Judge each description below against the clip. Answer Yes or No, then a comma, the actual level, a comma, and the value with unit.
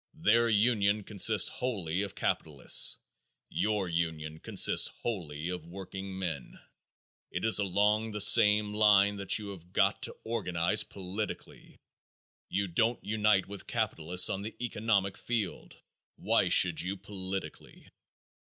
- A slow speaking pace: Yes, slow, 125 wpm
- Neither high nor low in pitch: No, low, 100 Hz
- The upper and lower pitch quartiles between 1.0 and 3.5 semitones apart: Yes, average, 2.9 semitones